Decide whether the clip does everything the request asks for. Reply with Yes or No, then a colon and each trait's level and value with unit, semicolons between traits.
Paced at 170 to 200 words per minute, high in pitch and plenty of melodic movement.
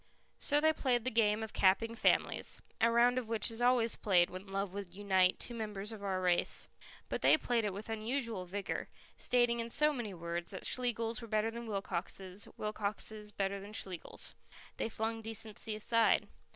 No: average, 180 wpm; high, 215 Hz; average, 2.9 semitones